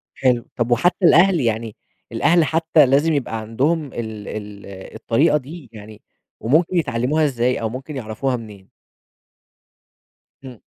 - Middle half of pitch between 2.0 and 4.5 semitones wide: No, wide, 5.6 semitones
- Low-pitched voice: Yes, low, 125 Hz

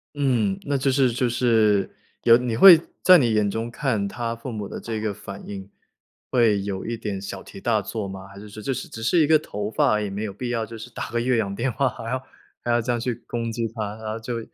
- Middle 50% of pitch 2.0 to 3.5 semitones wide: Yes, average, 2.8 semitones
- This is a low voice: Yes, low, 115 Hz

